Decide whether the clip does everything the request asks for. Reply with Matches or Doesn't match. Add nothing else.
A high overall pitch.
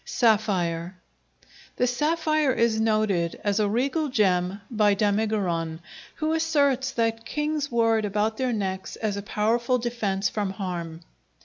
Matches